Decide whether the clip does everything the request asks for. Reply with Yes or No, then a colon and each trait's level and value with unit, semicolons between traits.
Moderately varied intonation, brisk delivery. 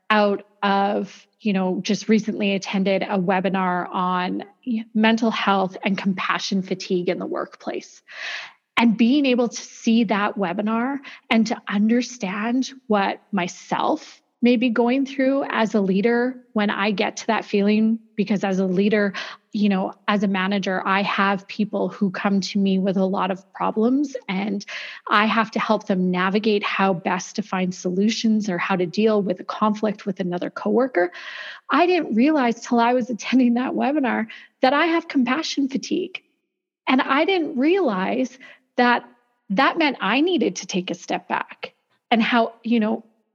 No: average, 3.9 semitones; average, 160 wpm